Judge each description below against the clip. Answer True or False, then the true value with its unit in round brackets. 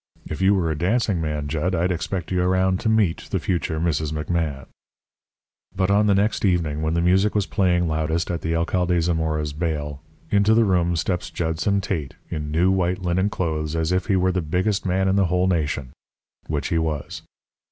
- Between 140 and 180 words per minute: False (195 wpm)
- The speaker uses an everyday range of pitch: True (3.0 semitones)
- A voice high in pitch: False (85 Hz)